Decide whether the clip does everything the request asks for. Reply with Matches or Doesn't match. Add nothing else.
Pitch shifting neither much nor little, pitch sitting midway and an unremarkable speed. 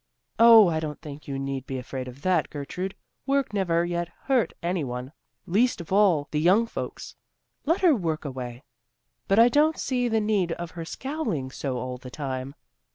Doesn't match